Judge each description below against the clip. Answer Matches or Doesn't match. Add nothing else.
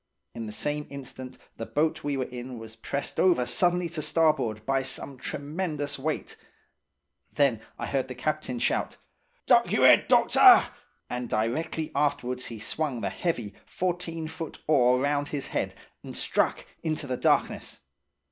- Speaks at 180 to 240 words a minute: Doesn't match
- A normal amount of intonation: Matches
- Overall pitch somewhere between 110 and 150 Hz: Matches